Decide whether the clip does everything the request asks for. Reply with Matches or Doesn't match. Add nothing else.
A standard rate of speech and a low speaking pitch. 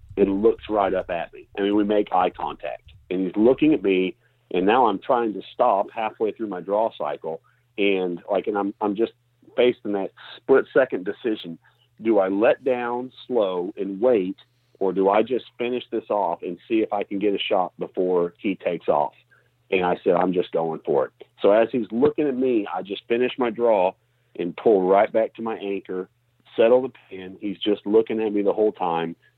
Doesn't match